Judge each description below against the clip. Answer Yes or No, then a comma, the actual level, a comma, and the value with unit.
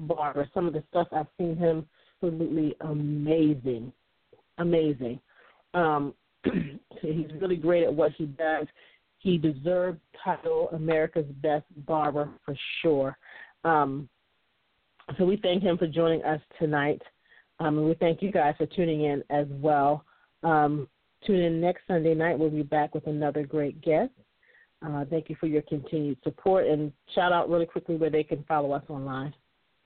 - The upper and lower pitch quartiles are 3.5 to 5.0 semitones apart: No, narrow, 2.5 semitones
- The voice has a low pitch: No, medium, 155 Hz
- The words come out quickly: No, average, 155 wpm